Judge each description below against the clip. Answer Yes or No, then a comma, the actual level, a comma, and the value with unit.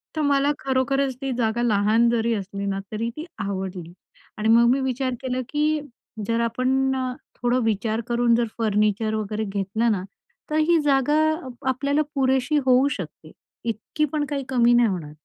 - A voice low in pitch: No, high, 235 Hz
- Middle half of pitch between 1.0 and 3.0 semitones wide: No, average, 3.7 semitones